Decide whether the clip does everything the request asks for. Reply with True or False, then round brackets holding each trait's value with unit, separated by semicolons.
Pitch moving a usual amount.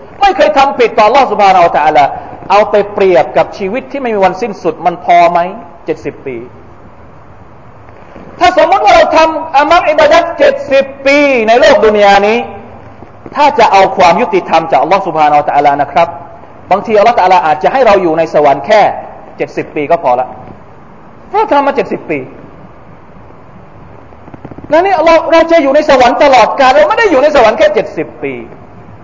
False (8.5 semitones)